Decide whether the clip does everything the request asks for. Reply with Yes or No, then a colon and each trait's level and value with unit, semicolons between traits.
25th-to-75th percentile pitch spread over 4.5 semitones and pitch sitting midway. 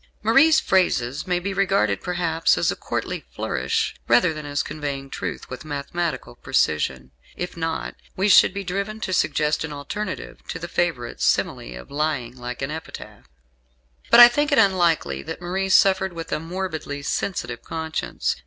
Yes: average, 5.1 semitones; medium, 165 Hz